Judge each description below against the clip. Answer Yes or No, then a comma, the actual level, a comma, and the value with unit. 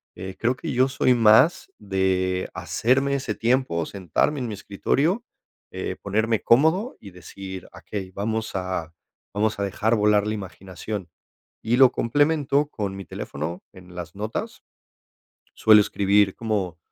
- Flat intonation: No, average, 4.7 semitones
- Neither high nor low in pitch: No, low, 105 Hz